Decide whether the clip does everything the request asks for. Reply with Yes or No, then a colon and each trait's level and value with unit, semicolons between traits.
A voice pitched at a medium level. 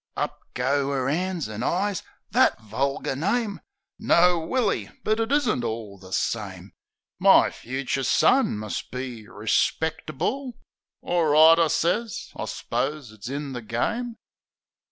Yes: medium, 145 Hz